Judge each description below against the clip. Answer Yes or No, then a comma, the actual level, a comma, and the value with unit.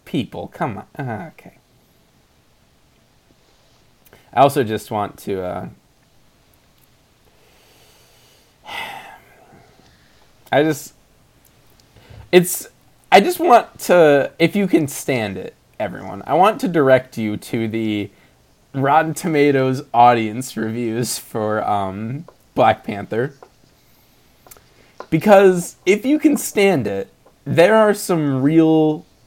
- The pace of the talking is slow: Yes, slow, 100 wpm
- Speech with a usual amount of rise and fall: No, wide, 6.7 semitones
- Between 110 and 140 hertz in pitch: Yes, low, 135 Hz